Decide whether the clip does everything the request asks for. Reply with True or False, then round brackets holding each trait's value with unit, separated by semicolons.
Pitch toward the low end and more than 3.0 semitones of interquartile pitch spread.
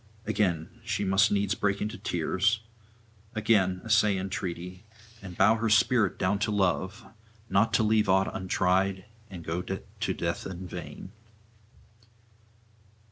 False (95 Hz; 2.4 semitones)